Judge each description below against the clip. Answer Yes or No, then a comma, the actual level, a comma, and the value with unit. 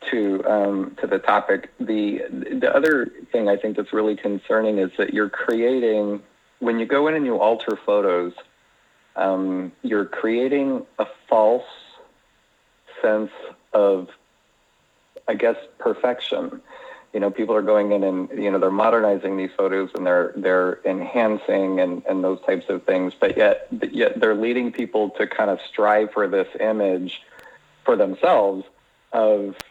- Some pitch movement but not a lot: No, narrow, 2.3 semitones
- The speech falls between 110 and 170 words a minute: Yes, average, 155 wpm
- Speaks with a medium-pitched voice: No, low, 105 Hz